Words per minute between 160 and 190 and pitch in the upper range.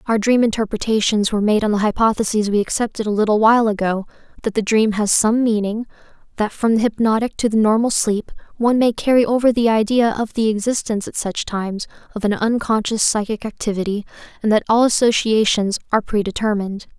Yes: average, 180 wpm; high, 215 Hz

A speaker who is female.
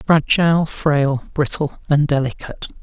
No: male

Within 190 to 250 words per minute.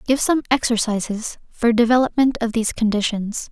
No: slow, 135 wpm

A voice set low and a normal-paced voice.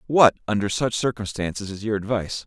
Yes: low, 105 Hz; average, 170 wpm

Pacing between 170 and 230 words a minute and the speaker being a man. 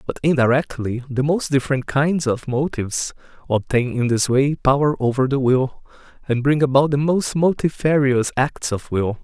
No: average, 160 wpm; male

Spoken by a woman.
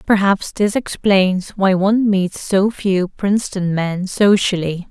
Yes: female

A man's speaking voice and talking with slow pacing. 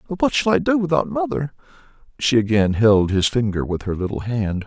No: male; fast, 205 wpm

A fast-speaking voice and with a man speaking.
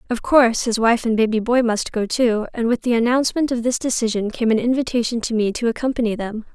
No: fast, 230 wpm; female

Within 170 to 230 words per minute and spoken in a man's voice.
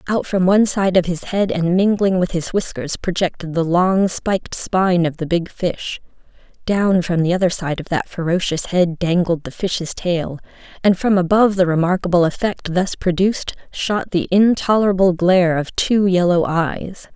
No: average, 175 wpm; female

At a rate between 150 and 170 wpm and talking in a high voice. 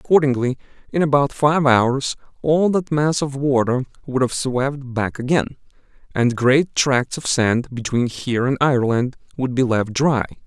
No: average, 160 wpm; low, 135 Hz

